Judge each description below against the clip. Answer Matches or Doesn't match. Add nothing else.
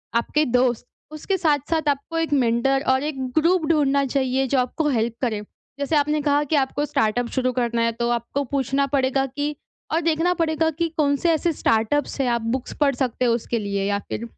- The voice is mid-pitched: Doesn't match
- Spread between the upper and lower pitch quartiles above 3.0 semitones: Matches